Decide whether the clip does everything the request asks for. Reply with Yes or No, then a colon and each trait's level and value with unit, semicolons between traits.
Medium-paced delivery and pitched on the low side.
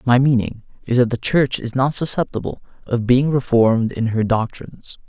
Yes: average, 175 wpm; low, 125 Hz